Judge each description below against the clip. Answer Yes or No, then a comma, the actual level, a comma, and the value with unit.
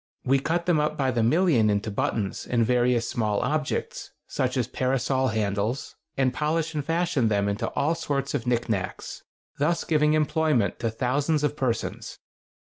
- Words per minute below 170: Yes, average, 160 wpm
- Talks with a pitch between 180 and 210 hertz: No, low, 130 Hz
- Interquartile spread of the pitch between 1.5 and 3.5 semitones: No, average, 4.9 semitones